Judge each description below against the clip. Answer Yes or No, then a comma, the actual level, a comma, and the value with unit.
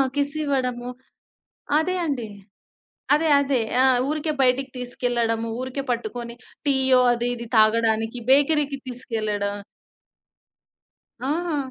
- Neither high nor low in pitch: No, very high, 250 Hz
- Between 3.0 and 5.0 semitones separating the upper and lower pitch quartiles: Yes, average, 3.3 semitones